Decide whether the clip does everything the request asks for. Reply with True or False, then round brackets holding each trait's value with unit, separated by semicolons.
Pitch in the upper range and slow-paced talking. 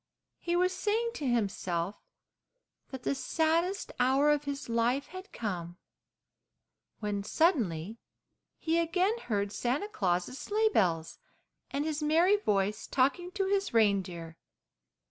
True (270 Hz; 125 wpm)